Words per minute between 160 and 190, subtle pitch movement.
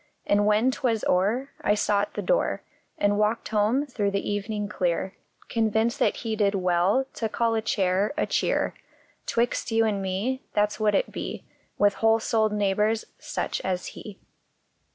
Yes: average, 185 wpm; narrow, 2.0 semitones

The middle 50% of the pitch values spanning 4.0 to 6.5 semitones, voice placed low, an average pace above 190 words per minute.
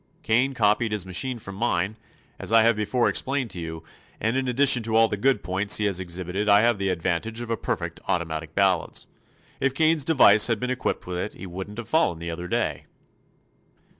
Yes: average, 4.6 semitones; low, 105 Hz; fast, 205 wpm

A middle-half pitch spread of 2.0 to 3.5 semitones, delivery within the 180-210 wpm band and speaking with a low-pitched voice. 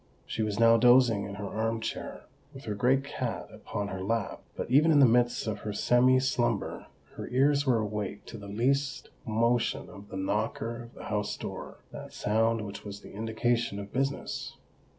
Yes: average, 3.1 semitones; average, 185 wpm; low, 115 Hz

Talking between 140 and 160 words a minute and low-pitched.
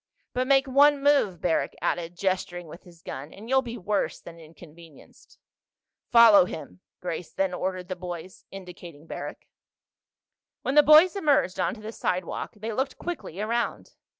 No: average, 150 wpm; medium, 185 Hz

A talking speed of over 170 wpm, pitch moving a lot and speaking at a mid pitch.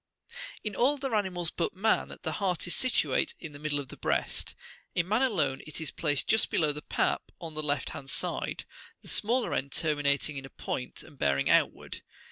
Yes: average, 200 wpm; wide, 6.3 semitones; medium, 160 Hz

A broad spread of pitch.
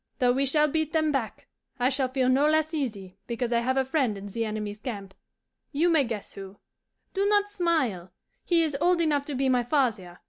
Yes: wide, 5.8 semitones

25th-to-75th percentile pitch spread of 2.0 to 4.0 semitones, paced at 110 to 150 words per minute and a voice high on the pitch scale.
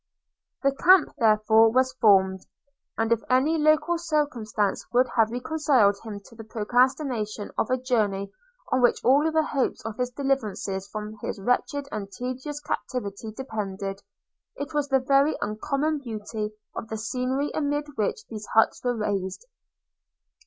No: average, 4.7 semitones; average, 145 wpm; high, 245 Hz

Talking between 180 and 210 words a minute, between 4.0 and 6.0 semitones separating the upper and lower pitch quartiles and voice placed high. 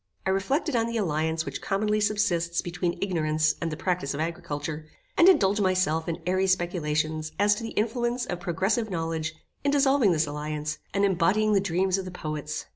No: average, 185 wpm; average, 4.6 semitones; medium, 180 Hz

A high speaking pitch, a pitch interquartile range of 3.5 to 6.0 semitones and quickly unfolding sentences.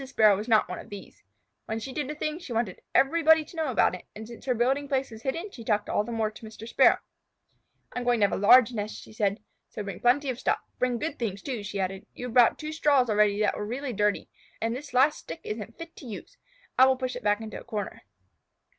Yes: high, 235 Hz; average, 4.2 semitones; fast, 250 wpm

